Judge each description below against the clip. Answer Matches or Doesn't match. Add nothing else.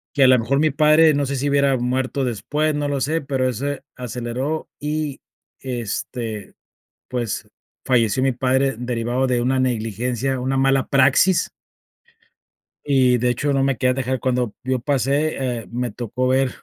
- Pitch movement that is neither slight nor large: Doesn't match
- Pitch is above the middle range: Doesn't match